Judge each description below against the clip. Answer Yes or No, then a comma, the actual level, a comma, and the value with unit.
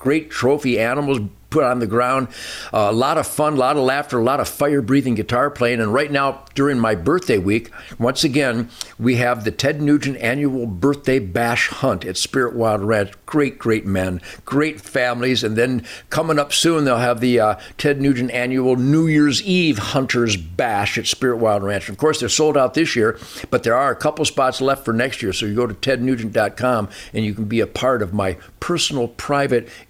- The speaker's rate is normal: No, fast, 210 wpm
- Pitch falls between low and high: No, low, 125 Hz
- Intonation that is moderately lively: Yes, average, 4.1 semitones